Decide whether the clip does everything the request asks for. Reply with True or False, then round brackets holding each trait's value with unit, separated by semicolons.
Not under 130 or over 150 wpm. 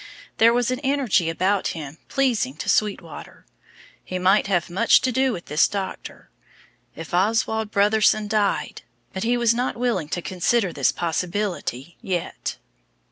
True (145 wpm)